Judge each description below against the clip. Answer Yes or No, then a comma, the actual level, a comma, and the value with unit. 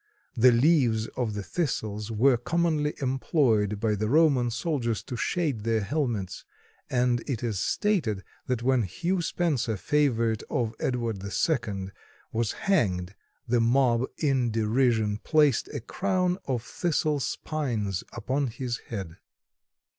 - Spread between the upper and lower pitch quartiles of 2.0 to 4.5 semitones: No, average, 4.9 semitones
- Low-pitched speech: Yes, low, 120 Hz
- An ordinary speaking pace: No, slow, 130 wpm